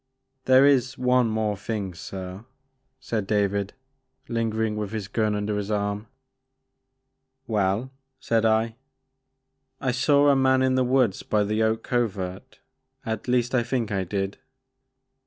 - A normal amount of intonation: Yes, average, 3.6 semitones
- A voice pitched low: Yes, low, 110 Hz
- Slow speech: Yes, slow, 130 wpm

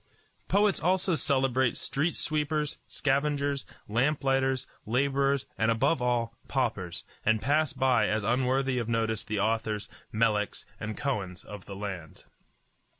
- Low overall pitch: Yes, low, 130 Hz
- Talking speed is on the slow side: Yes, slow, 130 wpm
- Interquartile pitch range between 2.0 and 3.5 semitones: No, average, 4.3 semitones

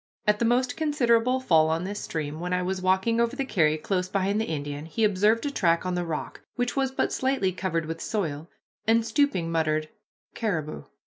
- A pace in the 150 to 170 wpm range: No, average, 200 wpm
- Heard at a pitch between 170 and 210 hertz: Yes, high, 190 Hz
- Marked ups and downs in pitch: Yes, wide, 6.0 semitones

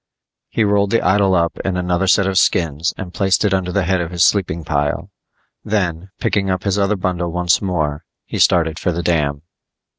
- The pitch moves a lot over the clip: No, narrow, 2.4 semitones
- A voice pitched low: Yes, very low, 90 Hz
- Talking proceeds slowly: No, average, 200 wpm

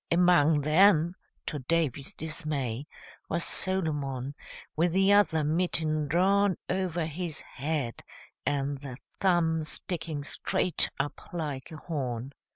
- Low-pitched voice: No, medium, 155 Hz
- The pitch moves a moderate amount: Yes, average, 3.5 semitones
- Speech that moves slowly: Yes, slow, 115 wpm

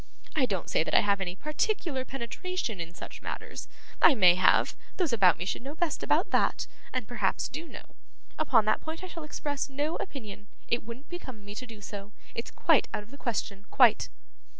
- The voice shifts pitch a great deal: Yes, wide, 6.4 semitones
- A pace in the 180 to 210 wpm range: Yes, average, 200 wpm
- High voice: Yes, high, 240 Hz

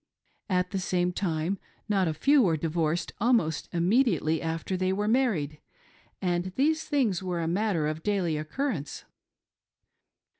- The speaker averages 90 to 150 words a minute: Yes, average, 140 wpm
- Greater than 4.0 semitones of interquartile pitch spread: Yes, average, 4.5 semitones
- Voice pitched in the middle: Yes, medium, 180 Hz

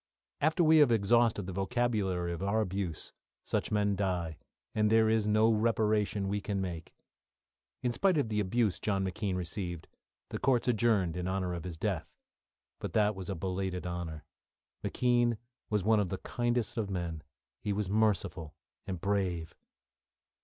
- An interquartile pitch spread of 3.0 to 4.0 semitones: Yes, average, 3.4 semitones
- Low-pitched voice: Yes, low, 100 Hz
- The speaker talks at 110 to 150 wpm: No, average, 160 wpm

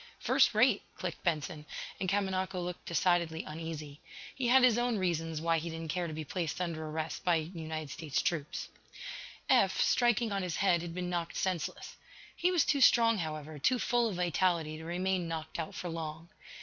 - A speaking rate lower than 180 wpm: No, average, 185 wpm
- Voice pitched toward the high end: No, medium, 170 Hz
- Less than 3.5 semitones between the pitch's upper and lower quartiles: Yes, average, 3.1 semitones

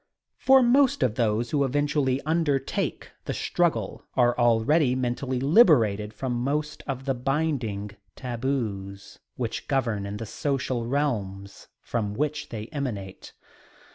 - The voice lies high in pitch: No, low, 130 Hz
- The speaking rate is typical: No, slow, 125 wpm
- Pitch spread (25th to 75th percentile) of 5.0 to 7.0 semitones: No, average, 4.6 semitones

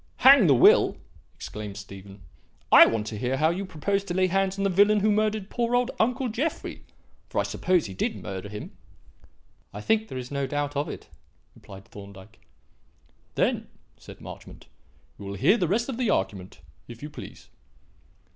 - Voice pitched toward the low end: No, medium, 160 Hz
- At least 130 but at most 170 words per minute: No, average, 180 wpm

